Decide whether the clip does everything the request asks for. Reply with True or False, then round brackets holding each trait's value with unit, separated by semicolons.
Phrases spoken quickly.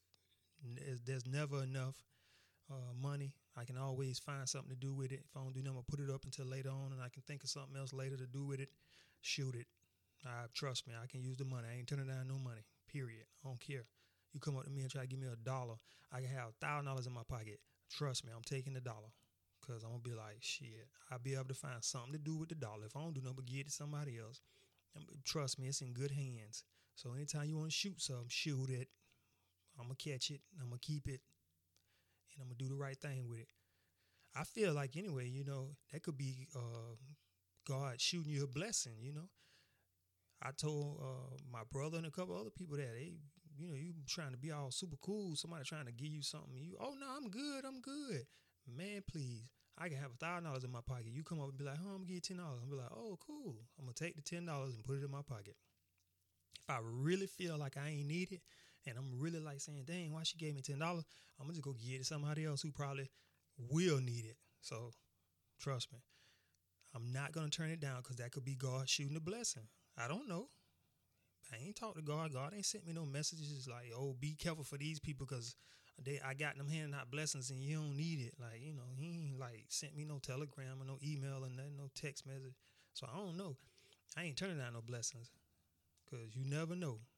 True (245 wpm)